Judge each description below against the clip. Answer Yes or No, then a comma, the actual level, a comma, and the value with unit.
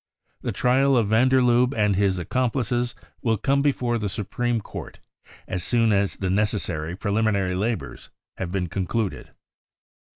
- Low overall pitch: Yes, low, 110 Hz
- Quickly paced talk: No, average, 150 wpm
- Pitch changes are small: No, average, 3.9 semitones